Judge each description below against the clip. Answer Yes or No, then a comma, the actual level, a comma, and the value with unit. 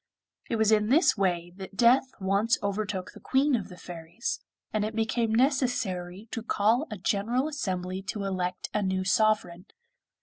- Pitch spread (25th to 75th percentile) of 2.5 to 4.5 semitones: Yes, average, 3.7 semitones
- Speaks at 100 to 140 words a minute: No, average, 165 wpm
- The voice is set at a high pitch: Yes, high, 210 Hz